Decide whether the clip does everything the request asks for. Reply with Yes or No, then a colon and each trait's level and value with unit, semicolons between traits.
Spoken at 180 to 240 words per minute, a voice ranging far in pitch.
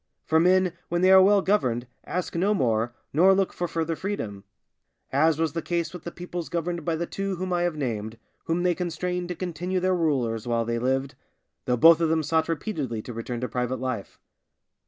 Yes: fast, 205 wpm; wide, 5.9 semitones